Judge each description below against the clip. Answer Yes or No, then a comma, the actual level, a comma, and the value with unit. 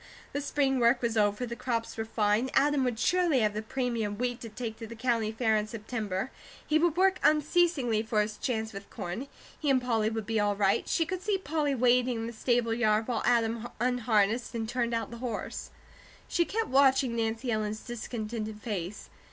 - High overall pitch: Yes, high, 235 Hz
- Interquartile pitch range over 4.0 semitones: No, average, 3.0 semitones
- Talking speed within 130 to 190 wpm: No, average, 200 wpm